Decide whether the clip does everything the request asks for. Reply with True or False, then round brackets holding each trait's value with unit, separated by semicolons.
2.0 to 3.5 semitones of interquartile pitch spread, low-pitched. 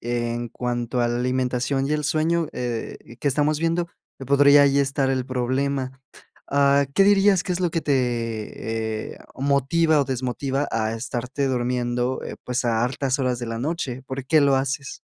True (2.7 semitones; 130 Hz)